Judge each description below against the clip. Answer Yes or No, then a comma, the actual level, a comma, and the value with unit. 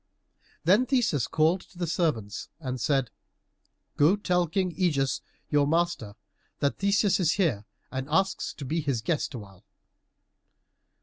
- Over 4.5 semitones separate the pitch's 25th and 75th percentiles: Yes, average, 5.3 semitones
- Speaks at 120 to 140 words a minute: Yes, slow, 135 wpm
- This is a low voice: No, medium, 155 Hz